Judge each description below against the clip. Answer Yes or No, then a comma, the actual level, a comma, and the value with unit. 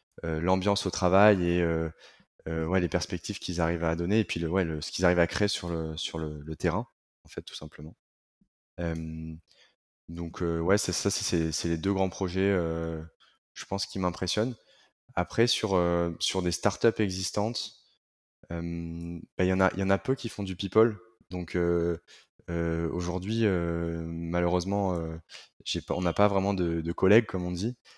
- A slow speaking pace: No, average, 190 wpm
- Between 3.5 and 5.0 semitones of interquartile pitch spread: No, average, 2.8 semitones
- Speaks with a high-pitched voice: No, very low, 90 Hz